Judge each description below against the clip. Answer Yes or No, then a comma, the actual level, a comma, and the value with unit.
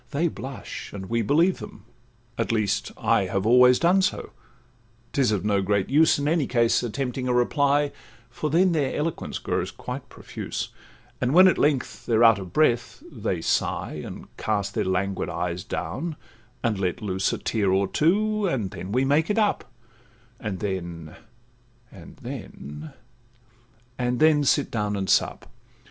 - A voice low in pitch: Yes, low, 120 Hz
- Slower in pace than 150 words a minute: No, average, 155 wpm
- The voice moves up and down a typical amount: No, wide, 6.2 semitones